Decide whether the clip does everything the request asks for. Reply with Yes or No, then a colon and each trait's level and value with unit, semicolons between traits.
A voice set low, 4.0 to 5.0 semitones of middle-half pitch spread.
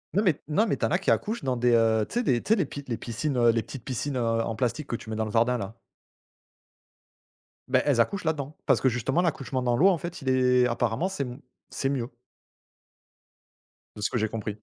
Yes: low, 125 Hz; average, 4.4 semitones